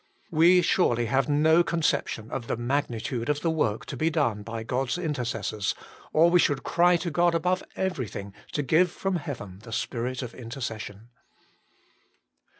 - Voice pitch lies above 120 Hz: Yes, low, 135 Hz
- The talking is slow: No, average, 160 wpm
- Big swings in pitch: Yes, wide, 6.3 semitones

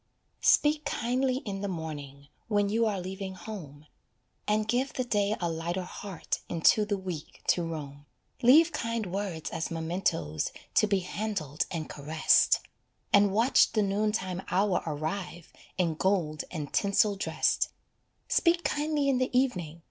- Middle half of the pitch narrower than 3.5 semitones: No, average, 4.9 semitones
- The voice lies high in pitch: Yes, high, 195 Hz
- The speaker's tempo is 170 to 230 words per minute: No, average, 150 wpm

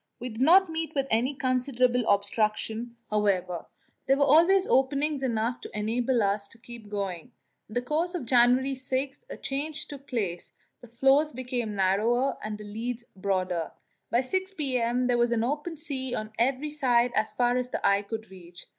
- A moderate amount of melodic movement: Yes, average, 4.0 semitones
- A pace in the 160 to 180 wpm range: Yes, average, 175 wpm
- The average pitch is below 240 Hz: No, high, 245 Hz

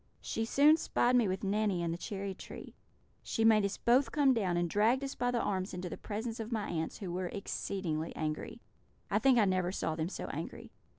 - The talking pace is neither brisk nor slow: No, fast, 220 wpm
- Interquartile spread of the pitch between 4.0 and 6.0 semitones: Yes, average, 4.6 semitones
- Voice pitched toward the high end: Yes, high, 200 Hz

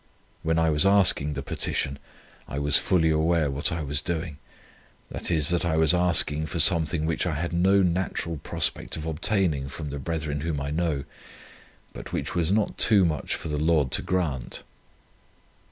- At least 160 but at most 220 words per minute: Yes, average, 180 wpm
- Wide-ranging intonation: No, average, 2.7 semitones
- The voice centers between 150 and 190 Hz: No, very low, 80 Hz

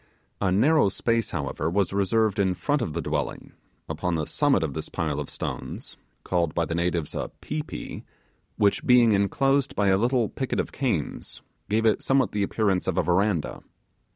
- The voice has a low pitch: Yes, low, 100 Hz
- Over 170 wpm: Yes, average, 180 wpm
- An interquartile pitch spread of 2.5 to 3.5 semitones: No, wide, 5.5 semitones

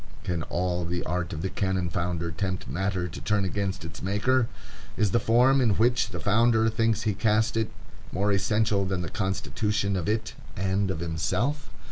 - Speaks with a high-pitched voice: No, low, 100 Hz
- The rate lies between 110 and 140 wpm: No, average, 180 wpm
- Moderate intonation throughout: Yes, average, 3.8 semitones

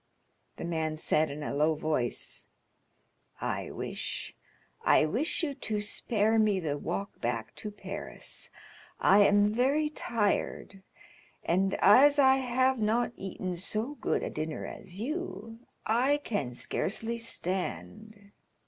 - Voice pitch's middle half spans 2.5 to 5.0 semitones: No, wide, 5.6 semitones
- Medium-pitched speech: No, high, 205 Hz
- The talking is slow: Yes, slow, 125 wpm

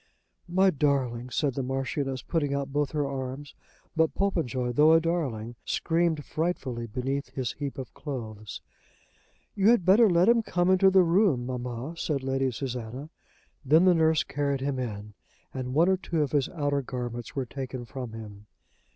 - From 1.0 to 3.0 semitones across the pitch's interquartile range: No, average, 4.5 semitones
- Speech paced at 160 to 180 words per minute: Yes, average, 170 wpm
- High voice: No, medium, 140 Hz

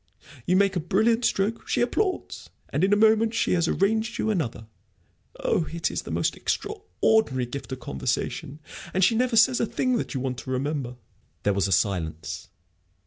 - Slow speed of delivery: No, average, 185 wpm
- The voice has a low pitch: No, medium, 185 Hz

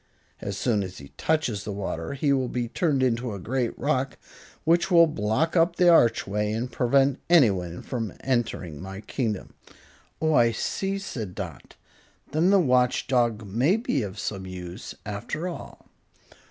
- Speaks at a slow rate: No, average, 160 wpm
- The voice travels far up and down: Yes, wide, 6.6 semitones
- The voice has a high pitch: No, low, 120 Hz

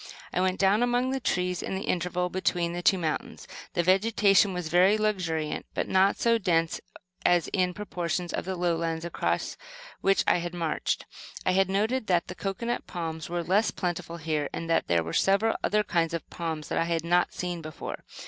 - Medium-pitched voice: Yes, medium, 180 Hz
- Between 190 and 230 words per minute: Yes, average, 195 wpm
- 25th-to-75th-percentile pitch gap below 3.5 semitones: Yes, narrow, 2.6 semitones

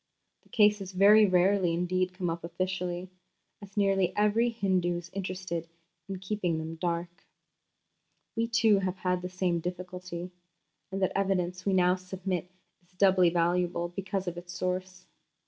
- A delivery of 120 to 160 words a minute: Yes, average, 145 wpm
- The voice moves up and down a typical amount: No, narrow, 1.7 semitones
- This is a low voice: No, medium, 185 Hz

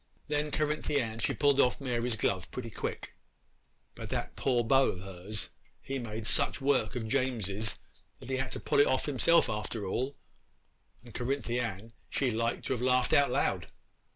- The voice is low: Yes, low, 125 Hz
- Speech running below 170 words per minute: No, average, 180 wpm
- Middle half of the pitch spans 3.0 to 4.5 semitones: Yes, average, 3.5 semitones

